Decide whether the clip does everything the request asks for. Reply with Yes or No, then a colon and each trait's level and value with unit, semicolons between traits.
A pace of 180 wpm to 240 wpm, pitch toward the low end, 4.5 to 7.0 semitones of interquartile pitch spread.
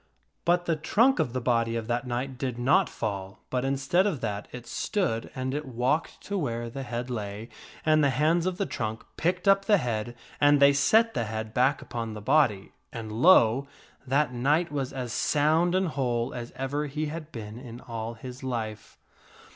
Yes: average, 195 wpm; low, 130 Hz; average, 4.8 semitones